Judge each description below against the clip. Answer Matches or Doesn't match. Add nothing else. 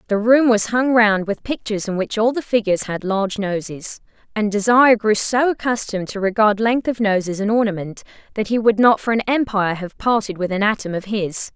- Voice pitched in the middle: Doesn't match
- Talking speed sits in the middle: Doesn't match